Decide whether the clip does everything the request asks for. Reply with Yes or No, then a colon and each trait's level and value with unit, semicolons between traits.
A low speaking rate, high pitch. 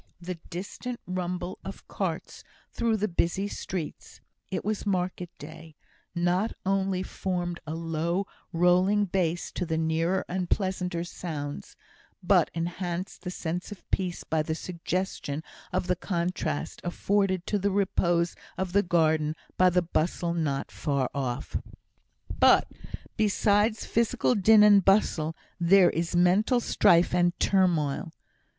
No: slow, 130 wpm; medium, 180 Hz